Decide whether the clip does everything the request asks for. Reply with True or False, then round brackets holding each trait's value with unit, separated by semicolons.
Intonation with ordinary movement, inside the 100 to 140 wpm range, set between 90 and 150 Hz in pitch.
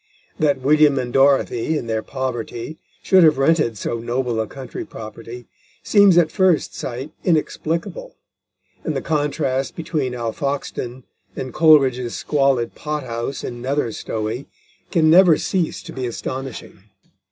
True (4.3 semitones; 135 wpm; 135 Hz)